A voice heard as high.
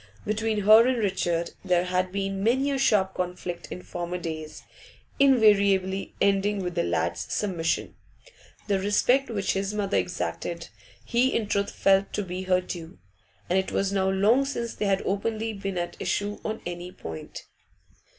Yes: high, 195 Hz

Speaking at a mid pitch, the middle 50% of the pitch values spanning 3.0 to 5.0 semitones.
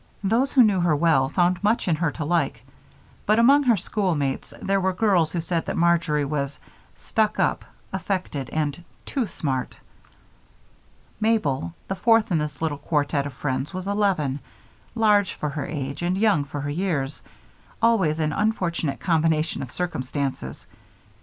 No: medium, 165 Hz; wide, 5.4 semitones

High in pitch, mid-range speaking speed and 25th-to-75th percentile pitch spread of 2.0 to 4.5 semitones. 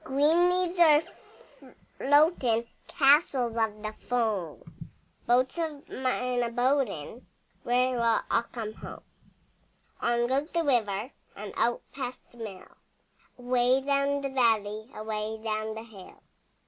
No: high, 245 Hz; slow, 125 wpm; average, 4.0 semitones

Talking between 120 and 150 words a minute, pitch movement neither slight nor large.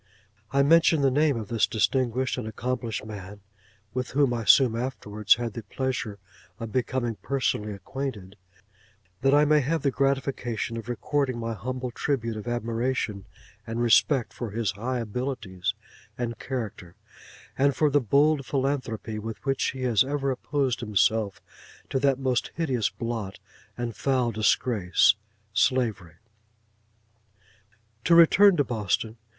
Yes: slow, 135 wpm; average, 3.7 semitones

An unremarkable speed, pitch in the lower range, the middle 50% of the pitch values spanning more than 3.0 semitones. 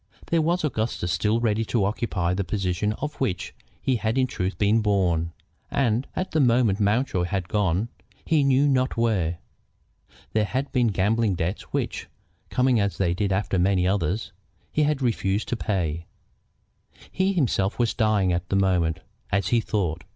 Yes: average, 165 wpm; low, 105 Hz; average, 4.6 semitones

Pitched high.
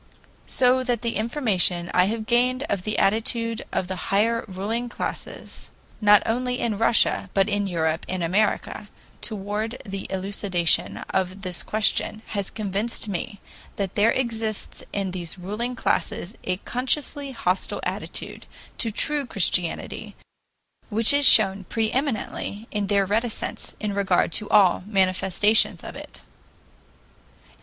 Yes: high, 210 Hz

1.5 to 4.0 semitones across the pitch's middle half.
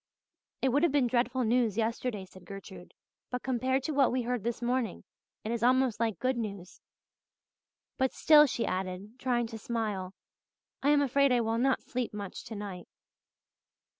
Yes: average, 3.6 semitones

